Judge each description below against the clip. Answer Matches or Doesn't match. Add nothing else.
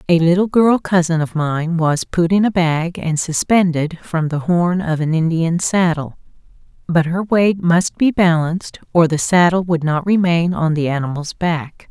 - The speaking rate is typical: Matches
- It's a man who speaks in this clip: Doesn't match